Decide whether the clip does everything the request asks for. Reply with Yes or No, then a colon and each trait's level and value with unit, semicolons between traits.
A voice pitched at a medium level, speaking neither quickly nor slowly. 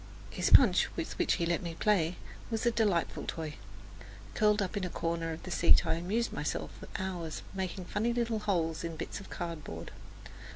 Yes: medium, 180 Hz; average, 190 wpm